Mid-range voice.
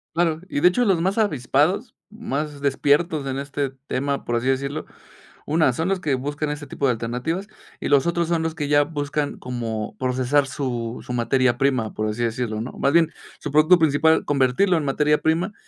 Yes: medium, 145 Hz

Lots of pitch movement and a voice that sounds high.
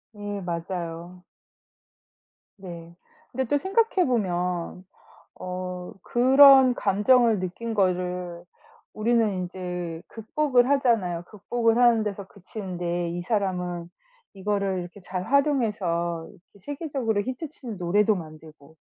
No: average, 5.0 semitones; high, 195 Hz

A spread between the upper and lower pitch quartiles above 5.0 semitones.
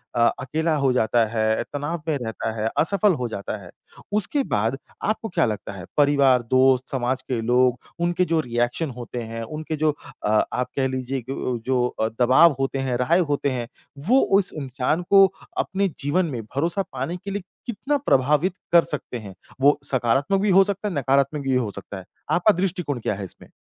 Yes: wide, 5.6 semitones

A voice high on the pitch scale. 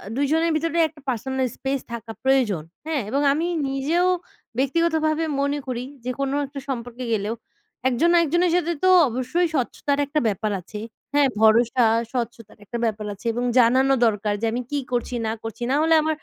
Yes: very high, 265 Hz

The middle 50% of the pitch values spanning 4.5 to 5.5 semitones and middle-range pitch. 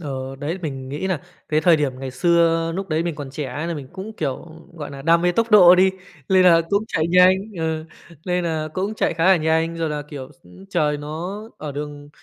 No: average, 3.4 semitones; medium, 160 Hz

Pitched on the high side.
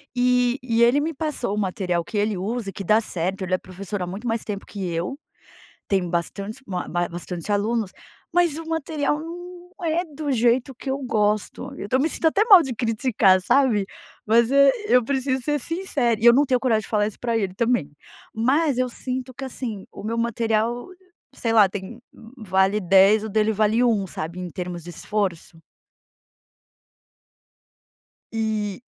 Yes: high, 225 Hz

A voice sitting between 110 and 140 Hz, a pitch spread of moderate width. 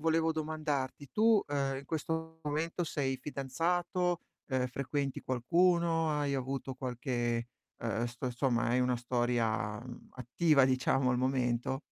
Yes: low, 135 Hz; average, 4.2 semitones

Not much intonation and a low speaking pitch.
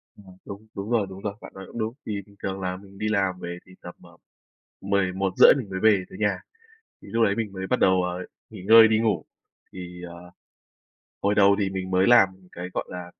Yes: narrow, 2.1 semitones; very low, 95 Hz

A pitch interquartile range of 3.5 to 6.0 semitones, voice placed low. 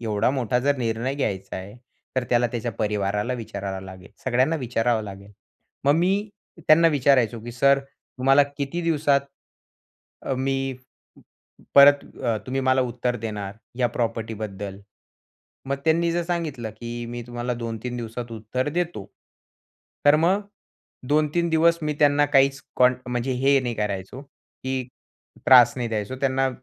Yes: average, 3.8 semitones; low, 125 Hz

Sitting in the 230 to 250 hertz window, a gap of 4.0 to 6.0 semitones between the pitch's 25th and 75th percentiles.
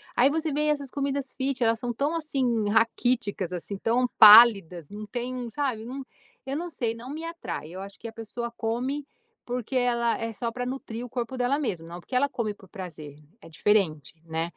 Yes: high, 235 Hz; average, 4.3 semitones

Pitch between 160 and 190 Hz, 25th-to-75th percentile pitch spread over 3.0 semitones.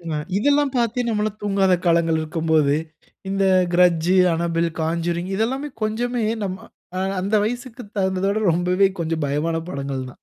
Yes: medium, 185 Hz; average, 4.7 semitones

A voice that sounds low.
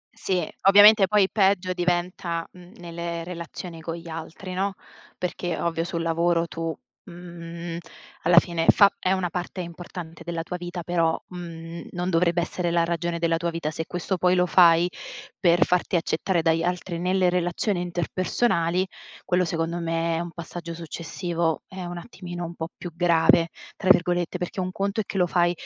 No: medium, 175 Hz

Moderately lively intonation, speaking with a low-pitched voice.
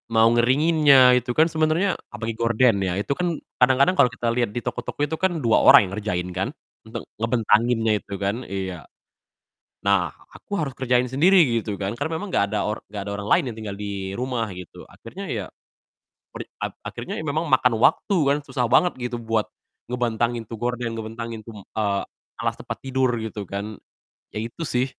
Yes: average, 3.7 semitones; low, 120 Hz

